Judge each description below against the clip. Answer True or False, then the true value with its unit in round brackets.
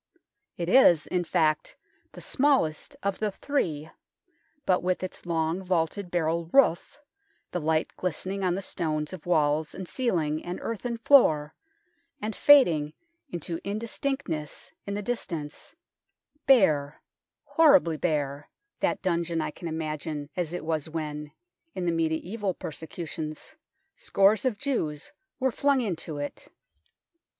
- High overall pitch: False (170 Hz)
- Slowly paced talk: True (130 wpm)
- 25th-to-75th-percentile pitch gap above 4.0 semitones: True (4.5 semitones)